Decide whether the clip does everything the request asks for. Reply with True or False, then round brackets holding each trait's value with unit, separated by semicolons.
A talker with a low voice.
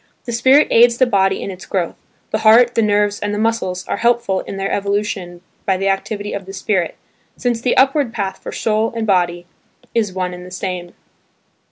False (205 Hz)